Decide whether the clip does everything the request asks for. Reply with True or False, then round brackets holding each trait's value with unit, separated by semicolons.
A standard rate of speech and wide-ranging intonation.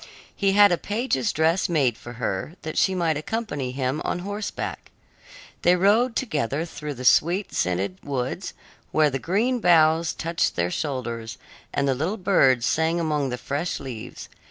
True (160 wpm; 5.9 semitones)